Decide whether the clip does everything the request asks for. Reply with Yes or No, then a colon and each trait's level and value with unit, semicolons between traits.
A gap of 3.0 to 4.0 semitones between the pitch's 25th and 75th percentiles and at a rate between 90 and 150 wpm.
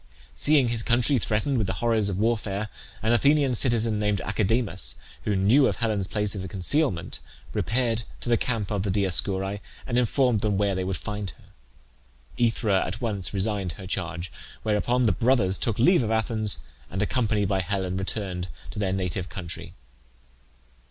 No: average, 3.4 semitones; average, 165 wpm